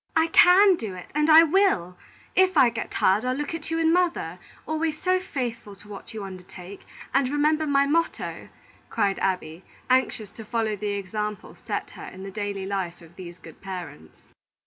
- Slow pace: No, average, 185 wpm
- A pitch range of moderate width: No, wide, 8.3 semitones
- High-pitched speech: Yes, high, 225 Hz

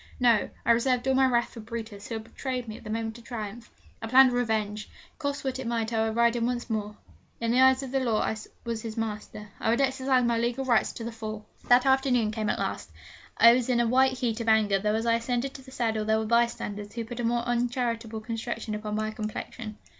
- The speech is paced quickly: Yes, fast, 245 wpm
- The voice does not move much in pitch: Yes, narrow, 2.1 semitones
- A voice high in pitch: Yes, high, 235 Hz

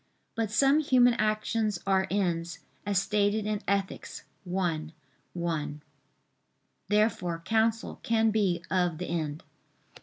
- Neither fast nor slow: No, slow, 115 wpm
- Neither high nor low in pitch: No, high, 200 Hz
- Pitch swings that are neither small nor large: Yes, average, 4.1 semitones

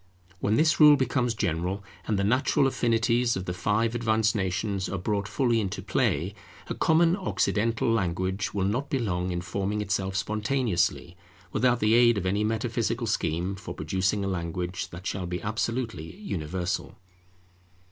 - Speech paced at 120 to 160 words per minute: Yes, average, 155 wpm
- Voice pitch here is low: Yes, low, 105 Hz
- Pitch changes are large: No, average, 4.0 semitones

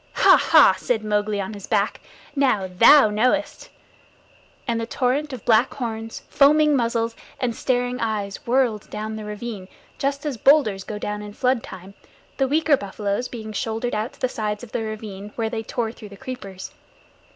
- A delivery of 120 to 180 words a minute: Yes, average, 175 wpm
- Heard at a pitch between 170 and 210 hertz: No, high, 225 Hz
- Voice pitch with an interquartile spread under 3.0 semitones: No, average, 3.3 semitones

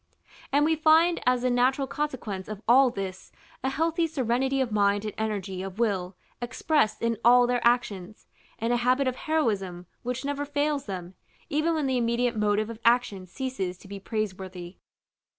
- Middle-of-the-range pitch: No, high, 240 Hz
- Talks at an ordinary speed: Yes, average, 170 wpm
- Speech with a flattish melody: No, average, 5.1 semitones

